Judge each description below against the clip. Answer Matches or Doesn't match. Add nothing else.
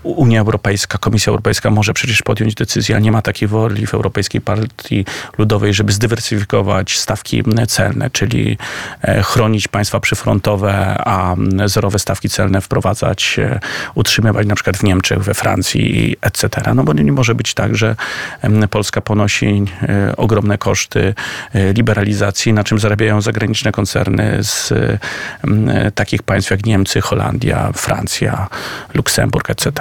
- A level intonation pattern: Matches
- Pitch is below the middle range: Matches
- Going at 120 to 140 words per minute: Matches